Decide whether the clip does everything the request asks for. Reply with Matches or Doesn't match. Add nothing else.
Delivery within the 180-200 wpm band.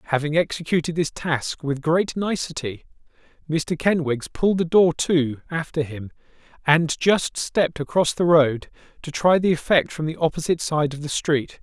Doesn't match